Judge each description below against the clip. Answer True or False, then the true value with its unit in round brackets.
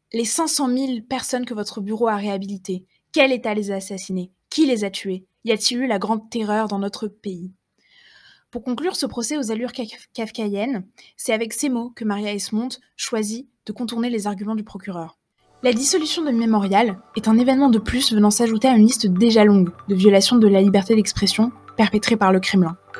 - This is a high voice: True (220 Hz)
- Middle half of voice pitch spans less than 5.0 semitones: True (3.3 semitones)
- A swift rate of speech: False (195 wpm)